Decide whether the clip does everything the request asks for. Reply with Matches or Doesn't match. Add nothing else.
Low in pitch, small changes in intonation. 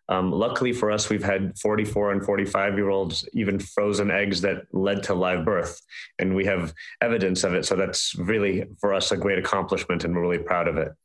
Matches